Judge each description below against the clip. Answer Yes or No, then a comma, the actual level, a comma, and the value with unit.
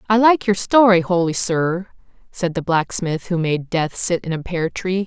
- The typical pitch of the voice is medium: Yes, medium, 180 Hz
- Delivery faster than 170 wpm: Yes, average, 200 wpm